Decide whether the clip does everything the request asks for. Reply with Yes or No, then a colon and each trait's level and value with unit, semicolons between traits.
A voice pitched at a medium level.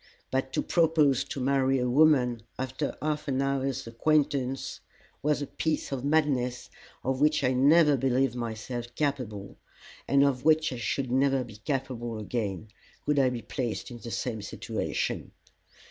No: low, 130 Hz